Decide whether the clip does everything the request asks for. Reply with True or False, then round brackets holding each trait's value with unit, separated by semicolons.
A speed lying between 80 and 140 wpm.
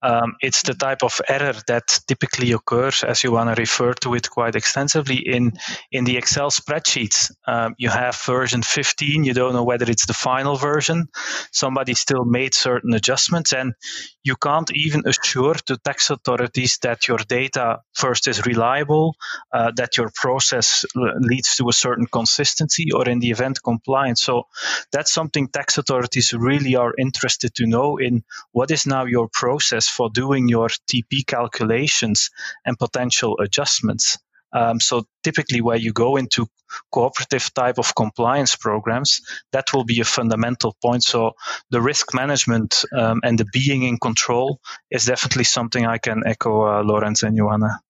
False (165 wpm)